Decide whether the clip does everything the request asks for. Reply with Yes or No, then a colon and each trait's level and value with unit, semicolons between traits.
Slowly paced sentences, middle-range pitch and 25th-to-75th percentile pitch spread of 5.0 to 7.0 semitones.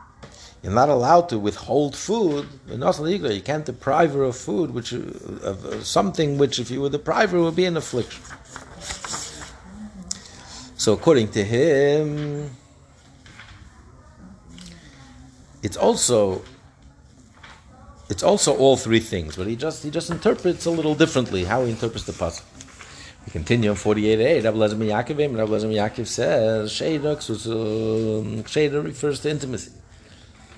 No: slow, 130 wpm; low, 125 Hz; wide, 5.5 semitones